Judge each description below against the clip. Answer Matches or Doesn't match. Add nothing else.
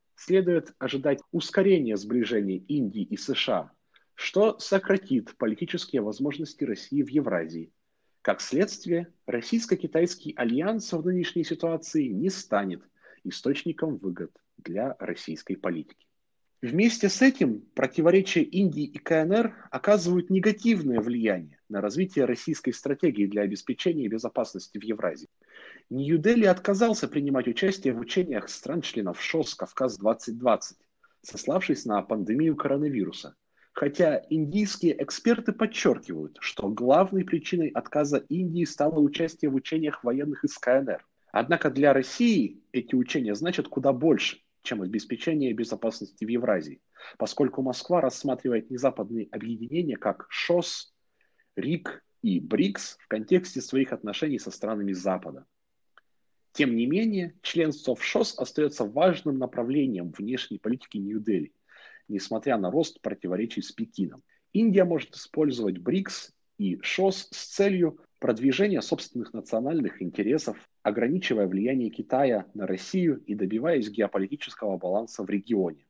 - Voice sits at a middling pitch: Matches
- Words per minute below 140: Matches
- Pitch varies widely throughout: Matches